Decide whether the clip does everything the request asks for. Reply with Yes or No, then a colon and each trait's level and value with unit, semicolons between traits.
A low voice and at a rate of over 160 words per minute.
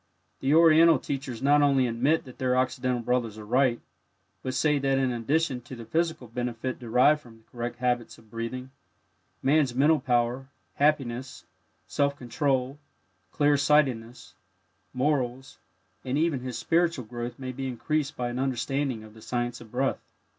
No: low, 130 Hz; average, 155 wpm